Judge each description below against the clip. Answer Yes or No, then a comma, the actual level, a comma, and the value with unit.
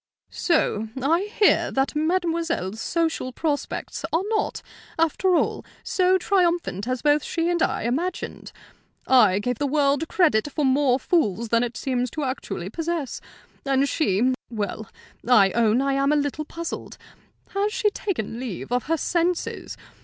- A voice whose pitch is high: Yes, very high, 285 Hz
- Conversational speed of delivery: Yes, average, 150 wpm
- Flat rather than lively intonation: No, wide, 5.6 semitones